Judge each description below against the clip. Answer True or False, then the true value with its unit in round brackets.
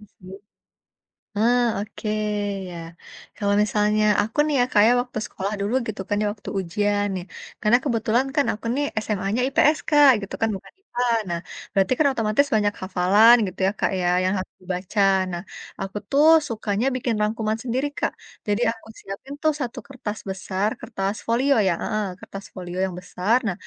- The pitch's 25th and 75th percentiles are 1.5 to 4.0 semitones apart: True (3.6 semitones)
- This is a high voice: True (210 Hz)